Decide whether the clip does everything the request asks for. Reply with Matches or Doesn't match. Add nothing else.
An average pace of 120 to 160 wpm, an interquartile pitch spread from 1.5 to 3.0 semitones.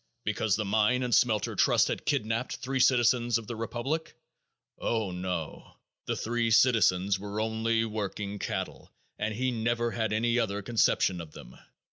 Matches